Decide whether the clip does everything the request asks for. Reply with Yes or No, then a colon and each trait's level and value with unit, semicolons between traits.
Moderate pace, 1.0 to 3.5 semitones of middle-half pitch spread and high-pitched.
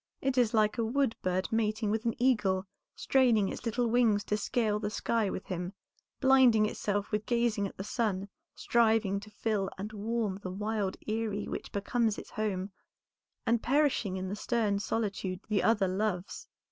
Yes: average, 170 wpm; narrow, 2.5 semitones; high, 215 Hz